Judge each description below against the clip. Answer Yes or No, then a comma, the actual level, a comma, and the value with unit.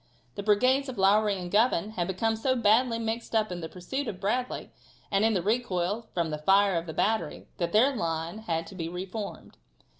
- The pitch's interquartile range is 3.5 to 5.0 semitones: Yes, average, 4.2 semitones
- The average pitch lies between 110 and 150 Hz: No, high, 205 Hz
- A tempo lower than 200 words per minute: No, fast, 205 wpm